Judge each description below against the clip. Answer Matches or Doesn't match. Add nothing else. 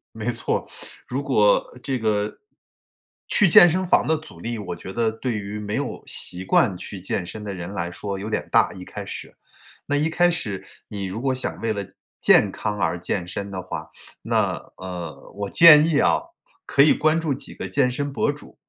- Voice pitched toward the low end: Matches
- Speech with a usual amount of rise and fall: Doesn't match